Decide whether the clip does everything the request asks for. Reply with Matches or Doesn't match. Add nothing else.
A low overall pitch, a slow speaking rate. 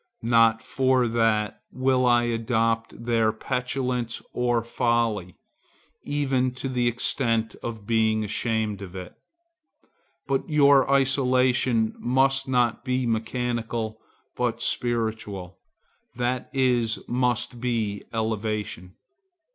Matches